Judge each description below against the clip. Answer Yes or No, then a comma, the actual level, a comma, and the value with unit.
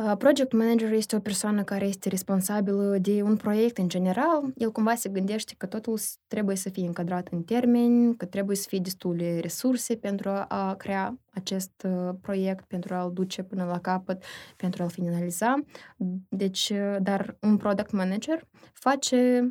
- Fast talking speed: No, average, 155 wpm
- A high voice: Yes, high, 200 Hz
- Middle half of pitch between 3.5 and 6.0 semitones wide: No, average, 3.0 semitones